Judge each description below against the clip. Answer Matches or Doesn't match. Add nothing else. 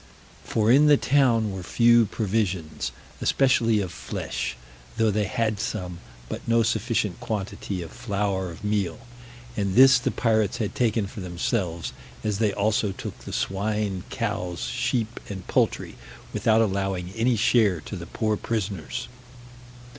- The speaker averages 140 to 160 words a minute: Matches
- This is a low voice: Matches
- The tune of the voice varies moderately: Matches